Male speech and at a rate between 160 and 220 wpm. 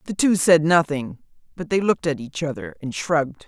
No: female; fast, 205 wpm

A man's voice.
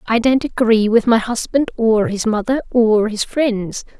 No: female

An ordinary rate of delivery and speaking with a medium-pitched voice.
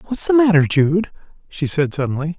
Yes: average, 175 wpm; medium, 170 Hz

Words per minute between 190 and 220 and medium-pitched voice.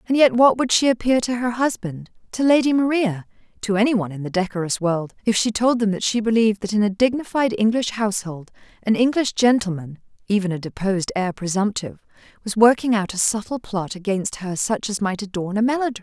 No: average, 200 wpm; high, 215 Hz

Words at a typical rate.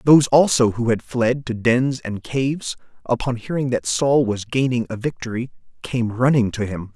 Yes: average, 180 wpm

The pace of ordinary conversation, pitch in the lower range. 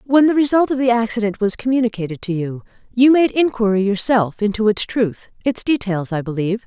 No: average, 190 wpm; high, 220 Hz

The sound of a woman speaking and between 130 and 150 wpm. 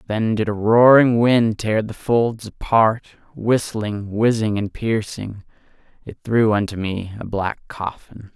No: male; average, 145 wpm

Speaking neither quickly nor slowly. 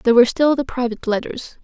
No: fast, 220 wpm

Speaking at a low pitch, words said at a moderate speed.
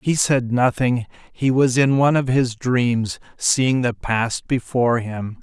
Yes: low, 125 Hz; average, 165 wpm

